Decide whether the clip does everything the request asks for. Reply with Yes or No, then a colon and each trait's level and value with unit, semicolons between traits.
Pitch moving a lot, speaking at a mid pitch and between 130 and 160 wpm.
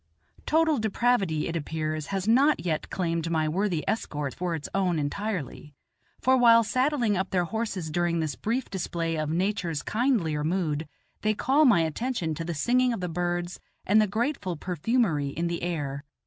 No: wide, 5.8 semitones; medium, 180 Hz; average, 170 wpm